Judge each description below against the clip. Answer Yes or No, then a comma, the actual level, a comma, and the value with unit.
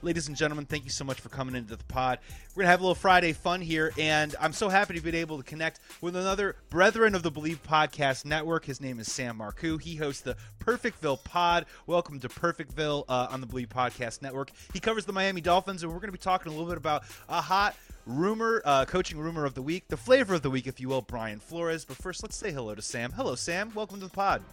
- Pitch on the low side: No, medium, 160 Hz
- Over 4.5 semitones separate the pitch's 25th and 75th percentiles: Yes, average, 5.2 semitones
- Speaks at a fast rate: Yes, fast, 255 wpm